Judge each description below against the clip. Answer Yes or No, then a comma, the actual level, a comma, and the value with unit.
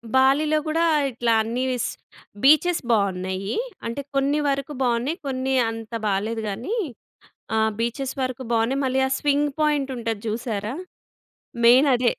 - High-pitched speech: Yes, very high, 255 Hz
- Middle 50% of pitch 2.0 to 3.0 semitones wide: No, average, 3.6 semitones